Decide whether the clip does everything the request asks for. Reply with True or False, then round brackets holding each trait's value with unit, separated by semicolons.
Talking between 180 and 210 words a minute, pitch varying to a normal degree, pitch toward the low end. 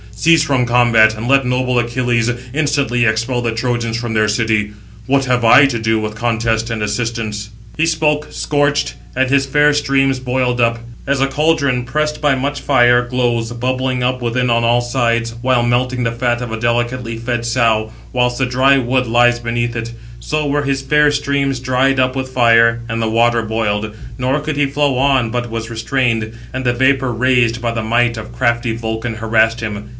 False (190 wpm; 2.3 semitones; 120 Hz)